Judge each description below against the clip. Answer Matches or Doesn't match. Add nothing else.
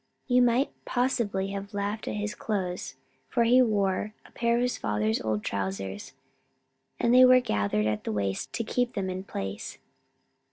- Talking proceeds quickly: Doesn't match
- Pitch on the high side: Matches